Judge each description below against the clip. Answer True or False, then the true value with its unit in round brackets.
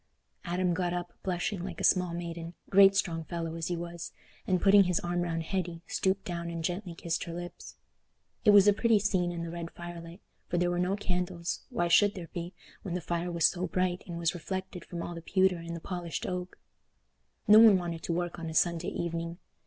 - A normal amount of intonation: False (1.6 semitones)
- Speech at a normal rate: False (210 wpm)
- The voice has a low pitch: False (175 Hz)